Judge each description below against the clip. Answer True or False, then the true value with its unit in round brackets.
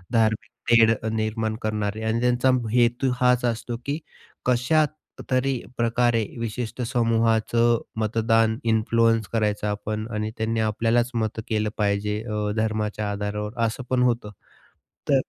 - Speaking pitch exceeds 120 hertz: False (115 Hz)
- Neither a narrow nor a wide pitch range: False (1.9 semitones)